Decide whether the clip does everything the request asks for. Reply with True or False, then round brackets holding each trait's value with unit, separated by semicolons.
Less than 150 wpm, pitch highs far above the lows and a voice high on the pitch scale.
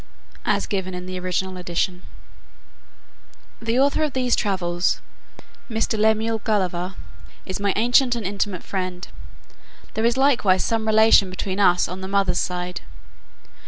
False (135 wpm; 3.4 semitones; 195 Hz)